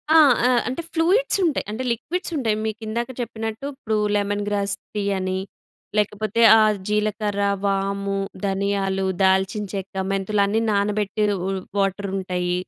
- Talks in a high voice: Yes, high, 205 Hz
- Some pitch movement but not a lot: No, narrow, 2.0 semitones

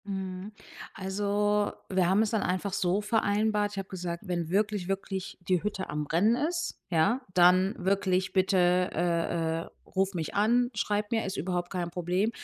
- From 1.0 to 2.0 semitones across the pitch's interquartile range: No, narrow, 2.5 semitones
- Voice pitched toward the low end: No, high, 190 Hz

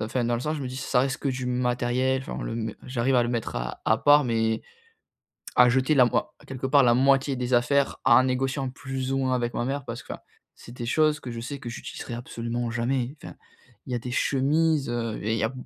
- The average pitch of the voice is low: Yes, low, 125 Hz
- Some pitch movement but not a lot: No, narrow, 2.2 semitones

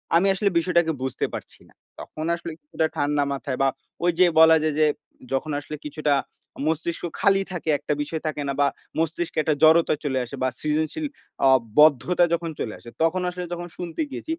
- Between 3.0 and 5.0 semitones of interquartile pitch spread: No, narrow, 2.6 semitones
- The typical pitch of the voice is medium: Yes, medium, 160 Hz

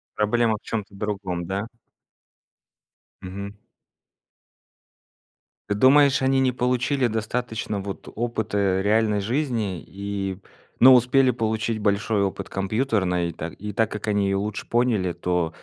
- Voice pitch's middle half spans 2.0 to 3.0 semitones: No, average, 3.5 semitones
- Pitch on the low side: Yes, low, 105 Hz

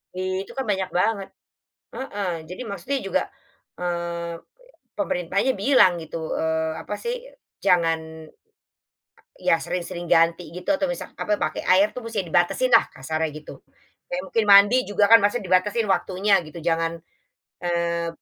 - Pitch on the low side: No, medium, 180 Hz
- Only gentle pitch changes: No, average, 3.6 semitones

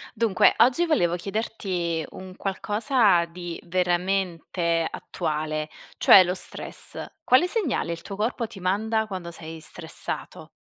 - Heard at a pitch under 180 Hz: No, medium, 185 Hz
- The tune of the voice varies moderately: Yes, average, 4.4 semitones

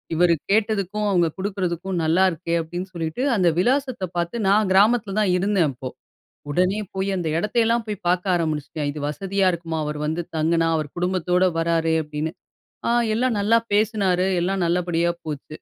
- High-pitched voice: No, medium, 180 Hz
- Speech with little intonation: No, average, 3.5 semitones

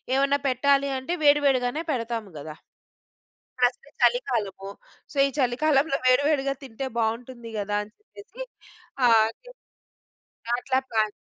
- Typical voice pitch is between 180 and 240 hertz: No, very high, 255 Hz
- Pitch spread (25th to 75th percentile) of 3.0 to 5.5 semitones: Yes, average, 3.7 semitones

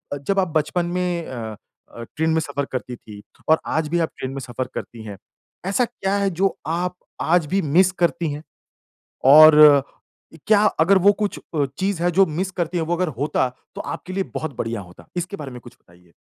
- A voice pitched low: No, medium, 160 Hz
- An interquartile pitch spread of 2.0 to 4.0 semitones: No, average, 5.3 semitones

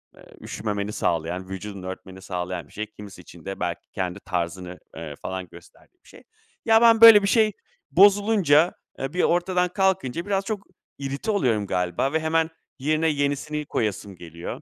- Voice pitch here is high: No, low, 115 Hz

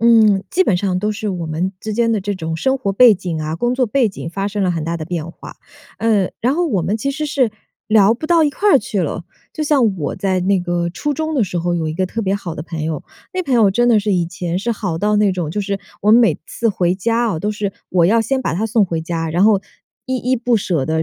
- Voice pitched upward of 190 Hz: Yes, high, 200 Hz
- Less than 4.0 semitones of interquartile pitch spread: No, average, 4.9 semitones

